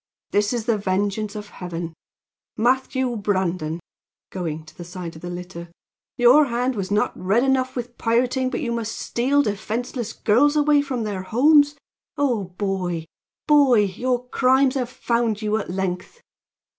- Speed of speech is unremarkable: Yes, average, 155 wpm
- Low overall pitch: No, high, 225 Hz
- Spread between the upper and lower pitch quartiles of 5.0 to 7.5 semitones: Yes, average, 5.3 semitones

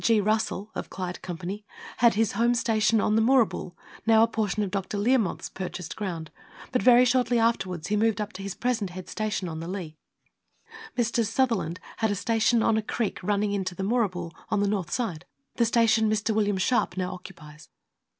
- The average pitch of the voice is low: No, high, 210 Hz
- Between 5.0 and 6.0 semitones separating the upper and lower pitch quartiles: No, average, 3.4 semitones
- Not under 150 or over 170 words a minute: No, average, 190 wpm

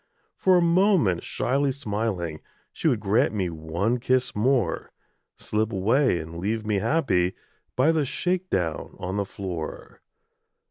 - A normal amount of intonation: No, wide, 7.3 semitones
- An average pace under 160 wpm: Yes, average, 140 wpm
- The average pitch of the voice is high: No, low, 110 Hz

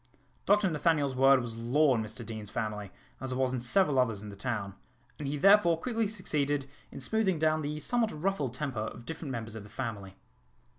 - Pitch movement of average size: No, wide, 5.8 semitones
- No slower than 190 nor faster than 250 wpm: Yes, average, 200 wpm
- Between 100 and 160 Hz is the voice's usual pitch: Yes, low, 135 Hz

